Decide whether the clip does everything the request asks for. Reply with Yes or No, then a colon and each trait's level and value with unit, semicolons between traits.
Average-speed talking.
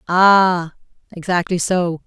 No: slow, 85 wpm